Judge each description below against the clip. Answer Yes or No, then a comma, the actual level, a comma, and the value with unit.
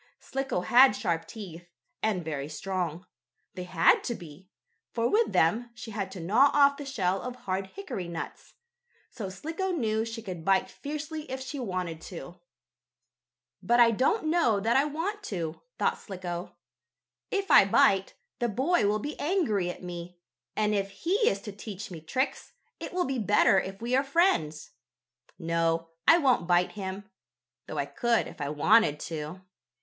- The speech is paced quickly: No, average, 170 wpm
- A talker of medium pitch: No, high, 200 Hz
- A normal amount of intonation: No, wide, 6.8 semitones